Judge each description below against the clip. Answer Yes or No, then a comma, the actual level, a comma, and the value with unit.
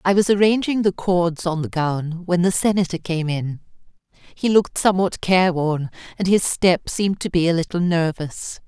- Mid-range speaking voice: Yes, medium, 180 Hz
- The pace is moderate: Yes, average, 180 wpm